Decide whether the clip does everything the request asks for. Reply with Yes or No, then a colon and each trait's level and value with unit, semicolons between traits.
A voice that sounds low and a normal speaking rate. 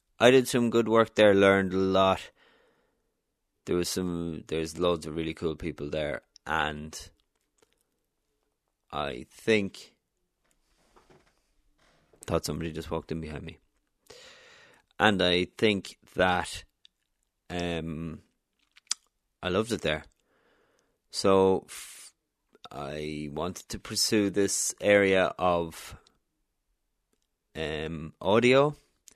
No: very low, 90 Hz; slow, 100 wpm